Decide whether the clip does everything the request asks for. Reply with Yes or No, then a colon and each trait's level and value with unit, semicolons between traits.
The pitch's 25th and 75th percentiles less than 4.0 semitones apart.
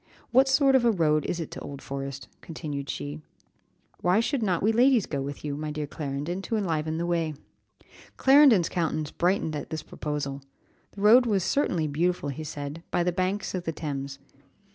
No: average, 5.2 semitones